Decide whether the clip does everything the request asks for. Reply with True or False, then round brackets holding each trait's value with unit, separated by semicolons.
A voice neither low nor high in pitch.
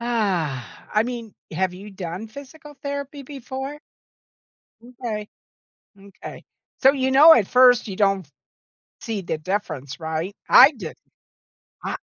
False (220 Hz)